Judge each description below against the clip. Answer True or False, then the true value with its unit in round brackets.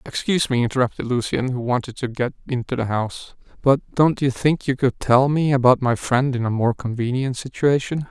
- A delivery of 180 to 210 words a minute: True (200 wpm)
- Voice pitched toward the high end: False (130 Hz)